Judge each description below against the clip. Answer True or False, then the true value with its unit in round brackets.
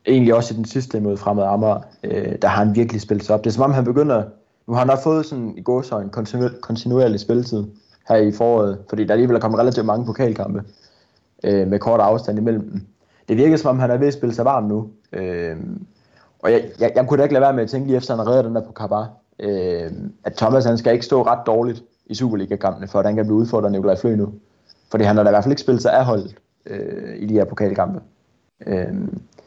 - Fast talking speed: True (250 wpm)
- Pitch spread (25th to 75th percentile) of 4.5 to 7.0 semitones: False (2.9 semitones)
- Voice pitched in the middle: False (110 Hz)